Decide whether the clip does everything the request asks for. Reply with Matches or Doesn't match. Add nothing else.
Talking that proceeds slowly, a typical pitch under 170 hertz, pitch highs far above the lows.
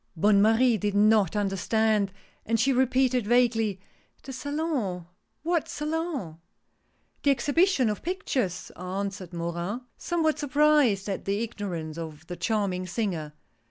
Doesn't match